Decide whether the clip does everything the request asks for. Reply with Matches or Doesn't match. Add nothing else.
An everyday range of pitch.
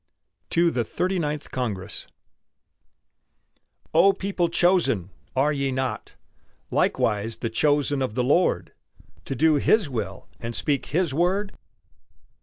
Doesn't match